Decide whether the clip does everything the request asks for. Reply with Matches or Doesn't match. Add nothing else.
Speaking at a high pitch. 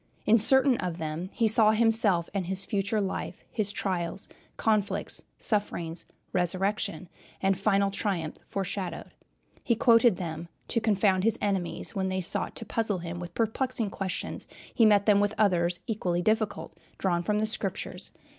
Matches